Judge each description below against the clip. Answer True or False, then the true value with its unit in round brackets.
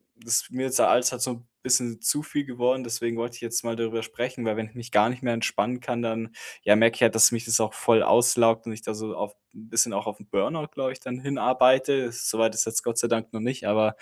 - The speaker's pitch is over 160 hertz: False (115 Hz)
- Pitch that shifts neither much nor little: False (2.0 semitones)